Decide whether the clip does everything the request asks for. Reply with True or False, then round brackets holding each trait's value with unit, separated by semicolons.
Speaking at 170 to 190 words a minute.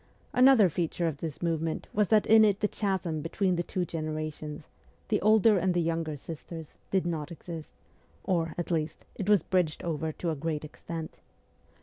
True (180 wpm)